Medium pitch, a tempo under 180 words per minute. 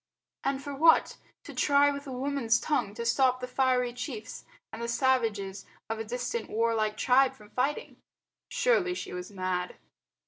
No: very high, 250 Hz; average, 165 wpm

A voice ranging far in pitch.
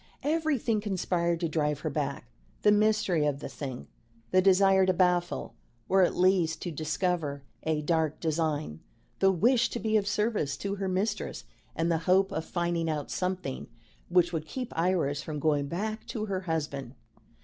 No: average, 4.1 semitones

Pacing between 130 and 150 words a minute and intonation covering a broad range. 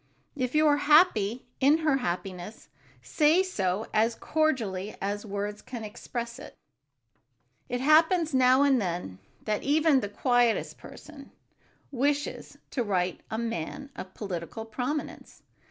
Yes: slow, 135 wpm; wide, 6.0 semitones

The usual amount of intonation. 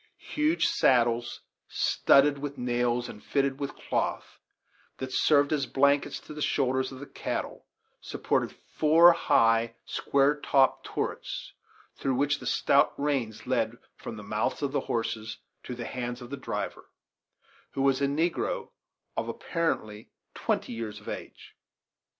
Yes: average, 3.1 semitones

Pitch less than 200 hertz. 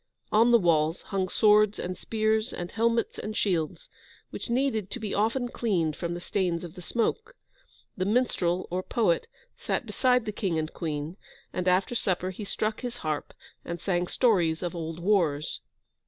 Yes: high, 190 Hz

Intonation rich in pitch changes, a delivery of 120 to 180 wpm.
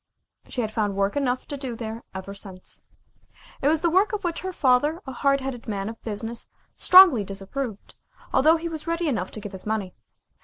No: wide, 6.8 semitones; average, 195 wpm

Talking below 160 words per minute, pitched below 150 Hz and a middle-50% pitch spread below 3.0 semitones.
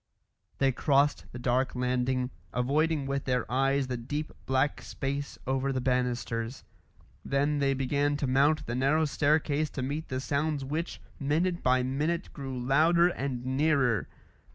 Yes: average, 150 wpm; low, 135 Hz; narrow, 2.4 semitones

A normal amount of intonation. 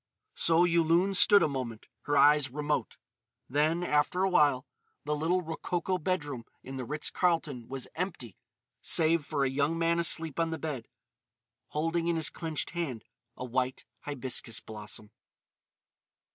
Yes: average, 3.9 semitones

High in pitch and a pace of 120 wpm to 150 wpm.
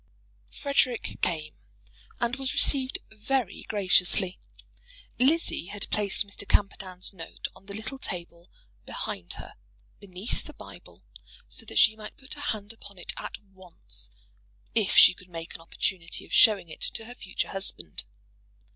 Yes: high, 200 Hz; average, 145 wpm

